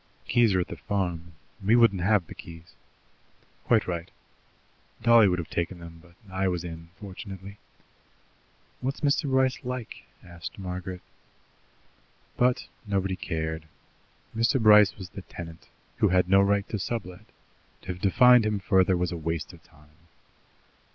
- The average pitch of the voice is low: Yes, very low, 95 Hz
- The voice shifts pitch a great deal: No, average, 3.8 semitones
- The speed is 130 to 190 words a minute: Yes, average, 150 wpm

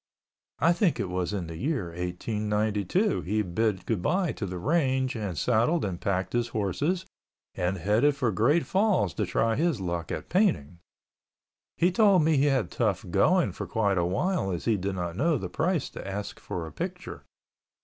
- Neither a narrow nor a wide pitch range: No, wide, 8.6 semitones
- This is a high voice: No, low, 110 Hz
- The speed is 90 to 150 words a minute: No, average, 180 wpm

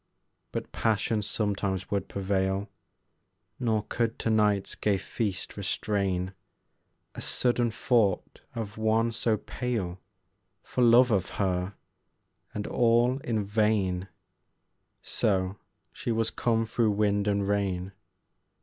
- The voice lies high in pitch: No, low, 105 Hz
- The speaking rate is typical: No, slow, 115 wpm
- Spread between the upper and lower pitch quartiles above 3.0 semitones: No, average, 2.7 semitones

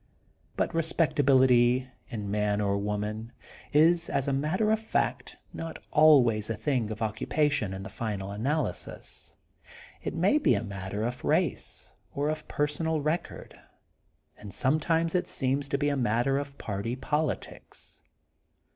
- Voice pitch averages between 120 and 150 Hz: Yes, low, 135 Hz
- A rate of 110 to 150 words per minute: Yes, average, 140 wpm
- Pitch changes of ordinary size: No, wide, 6.0 semitones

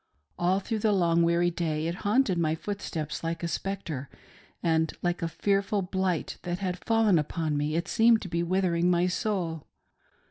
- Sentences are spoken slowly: No, average, 175 wpm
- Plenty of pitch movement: No, average, 2.9 semitones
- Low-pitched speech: No, medium, 175 Hz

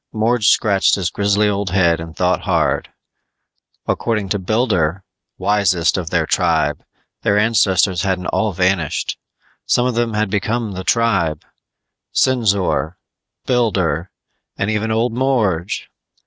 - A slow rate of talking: Yes, slow, 125 wpm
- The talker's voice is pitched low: Yes, low, 100 Hz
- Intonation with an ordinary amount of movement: Yes, average, 3.6 semitones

